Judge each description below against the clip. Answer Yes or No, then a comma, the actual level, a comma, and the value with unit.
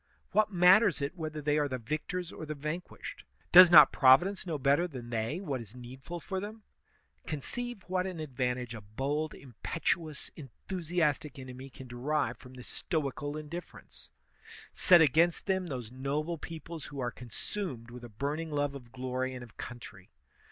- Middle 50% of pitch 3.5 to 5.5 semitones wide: Yes, average, 5.0 semitones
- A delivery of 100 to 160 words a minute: No, average, 175 wpm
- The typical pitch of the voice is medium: Yes, medium, 150 Hz